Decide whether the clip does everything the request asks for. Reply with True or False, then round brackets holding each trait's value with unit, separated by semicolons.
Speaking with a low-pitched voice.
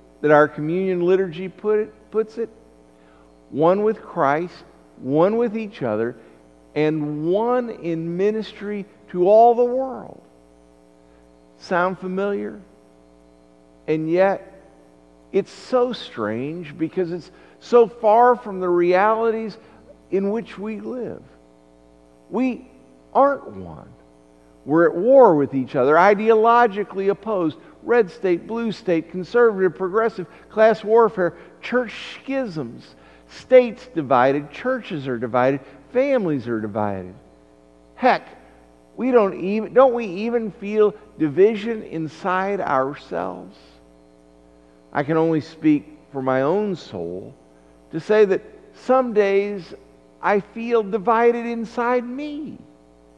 False (175 Hz)